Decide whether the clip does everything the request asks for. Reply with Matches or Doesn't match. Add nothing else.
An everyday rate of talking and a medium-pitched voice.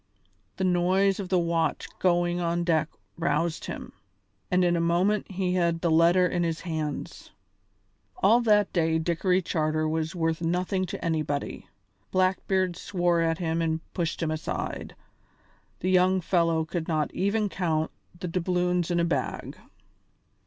Matches